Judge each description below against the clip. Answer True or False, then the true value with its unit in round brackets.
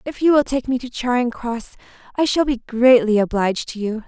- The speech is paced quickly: True (220 wpm)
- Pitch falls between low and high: False (245 Hz)